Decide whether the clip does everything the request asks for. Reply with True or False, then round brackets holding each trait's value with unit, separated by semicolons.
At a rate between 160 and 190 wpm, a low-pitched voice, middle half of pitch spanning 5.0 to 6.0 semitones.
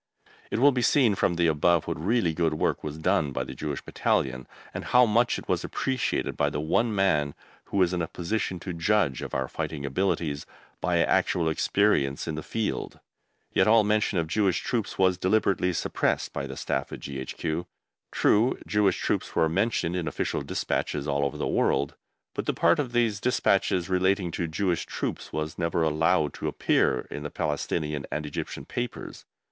True (185 wpm; 85 Hz; 5.3 semitones)